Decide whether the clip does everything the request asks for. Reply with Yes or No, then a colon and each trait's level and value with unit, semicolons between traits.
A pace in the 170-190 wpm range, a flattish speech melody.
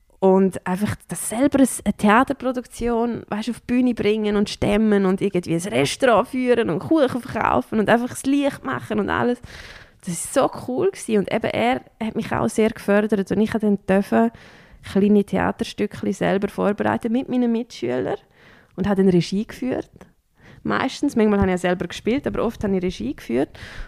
No: average, 175 wpm; average, 3.7 semitones